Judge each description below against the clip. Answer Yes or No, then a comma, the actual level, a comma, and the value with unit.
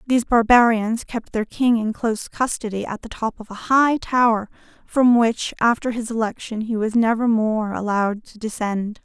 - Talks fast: No, average, 180 wpm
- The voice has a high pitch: Yes, high, 225 Hz